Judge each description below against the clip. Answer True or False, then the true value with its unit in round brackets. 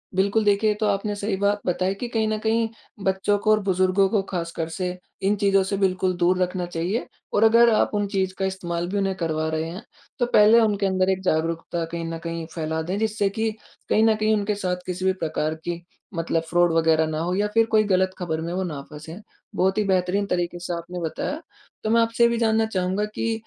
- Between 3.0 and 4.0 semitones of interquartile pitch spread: True (3.4 semitones)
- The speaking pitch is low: False (190 Hz)